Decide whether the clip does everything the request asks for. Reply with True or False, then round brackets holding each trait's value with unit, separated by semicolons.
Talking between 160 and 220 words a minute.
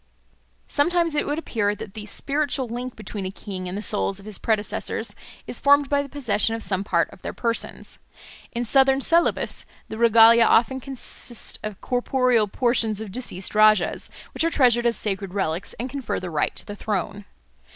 True (180 wpm)